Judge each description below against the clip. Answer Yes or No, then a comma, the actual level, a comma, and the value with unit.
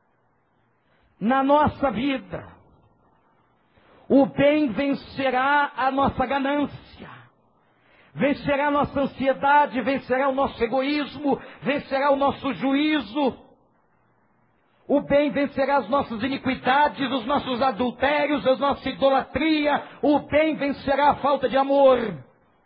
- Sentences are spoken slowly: Yes, slow, 105 wpm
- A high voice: Yes, very high, 275 Hz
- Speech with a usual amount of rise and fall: No, narrow, 1.3 semitones